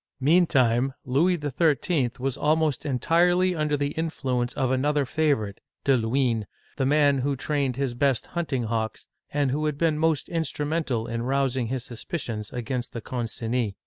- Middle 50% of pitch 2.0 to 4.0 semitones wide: Yes, average, 3.7 semitones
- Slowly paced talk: No, average, 165 wpm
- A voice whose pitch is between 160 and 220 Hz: No, low, 135 Hz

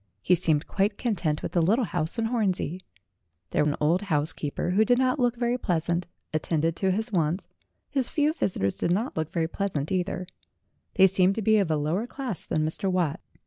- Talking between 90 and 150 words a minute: No, average, 195 wpm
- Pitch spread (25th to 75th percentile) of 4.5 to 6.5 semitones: Yes, wide, 5.4 semitones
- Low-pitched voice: No, medium, 185 Hz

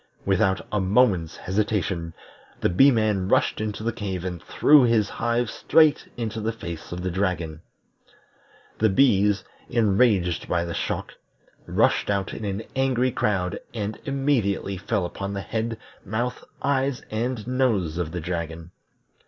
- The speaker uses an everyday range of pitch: Yes, average, 4.3 semitones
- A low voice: Yes, low, 105 Hz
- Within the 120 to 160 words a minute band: Yes, average, 145 wpm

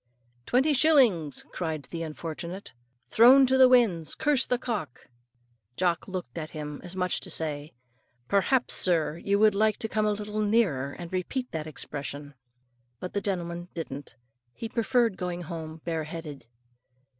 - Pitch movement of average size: No, wide, 5.7 semitones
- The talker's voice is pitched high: No, medium, 180 Hz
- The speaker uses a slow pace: No, average, 155 wpm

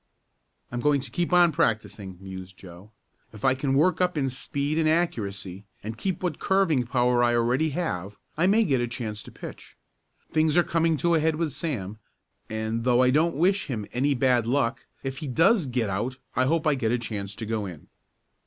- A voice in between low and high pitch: No, low, 130 Hz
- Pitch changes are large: Yes, wide, 6.2 semitones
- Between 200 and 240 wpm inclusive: Yes, fast, 205 wpm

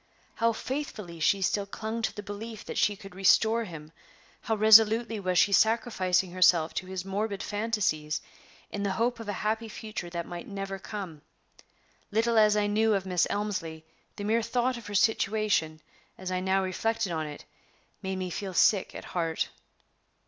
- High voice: Yes, high, 205 Hz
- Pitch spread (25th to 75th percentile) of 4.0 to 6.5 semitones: No, average, 3.2 semitones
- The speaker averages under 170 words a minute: No, average, 175 wpm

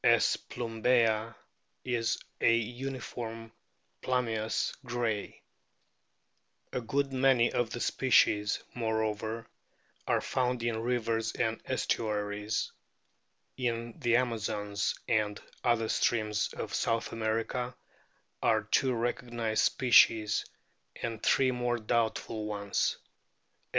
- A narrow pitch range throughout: Yes, narrow, 1.9 semitones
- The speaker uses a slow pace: Yes, slow, 100 wpm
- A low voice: Yes, low, 115 Hz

